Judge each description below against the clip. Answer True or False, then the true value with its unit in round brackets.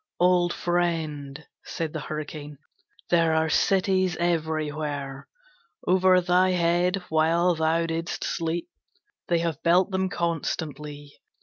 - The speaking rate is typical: False (110 wpm)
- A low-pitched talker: False (165 Hz)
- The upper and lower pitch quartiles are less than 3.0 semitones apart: True (2.4 semitones)